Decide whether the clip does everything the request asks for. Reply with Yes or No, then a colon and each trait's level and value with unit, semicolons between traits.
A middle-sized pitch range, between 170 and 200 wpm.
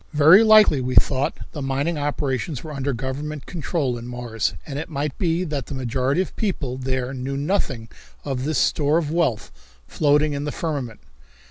Yes: average, 3.0 semitones; average, 185 wpm